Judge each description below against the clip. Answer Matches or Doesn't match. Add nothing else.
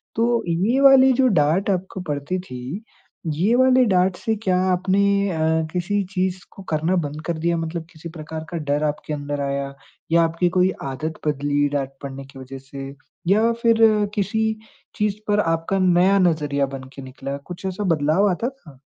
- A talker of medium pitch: Matches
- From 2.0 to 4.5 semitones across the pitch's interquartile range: Doesn't match